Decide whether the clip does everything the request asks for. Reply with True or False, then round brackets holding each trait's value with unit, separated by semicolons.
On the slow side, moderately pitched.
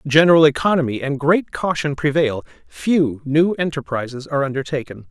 True (130 wpm; 145 Hz)